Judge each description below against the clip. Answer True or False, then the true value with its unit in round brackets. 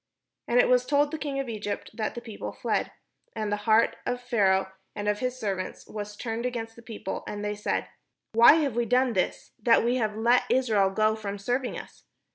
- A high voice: True (225 Hz)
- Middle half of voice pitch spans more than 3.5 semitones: False (3.1 semitones)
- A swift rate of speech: True (210 wpm)